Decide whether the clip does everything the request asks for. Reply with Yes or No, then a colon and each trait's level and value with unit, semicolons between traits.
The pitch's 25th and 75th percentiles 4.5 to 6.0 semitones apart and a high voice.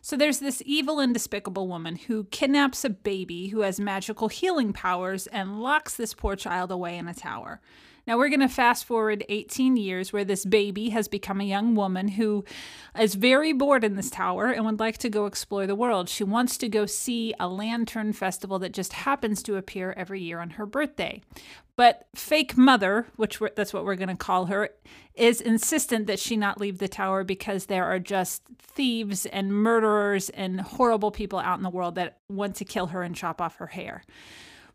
No: average, 3.8 semitones; high, 210 Hz